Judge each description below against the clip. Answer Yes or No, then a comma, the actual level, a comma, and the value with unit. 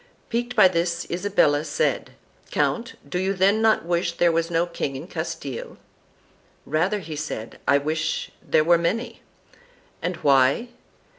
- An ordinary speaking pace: Yes, average, 150 wpm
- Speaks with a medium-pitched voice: Yes, medium, 170 Hz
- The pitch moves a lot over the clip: No, average, 3.8 semitones